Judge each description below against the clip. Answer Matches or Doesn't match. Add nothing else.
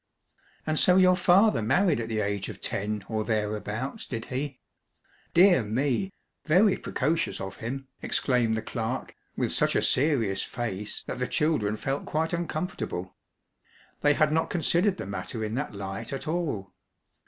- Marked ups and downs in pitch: Matches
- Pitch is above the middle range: Doesn't match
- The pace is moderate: Matches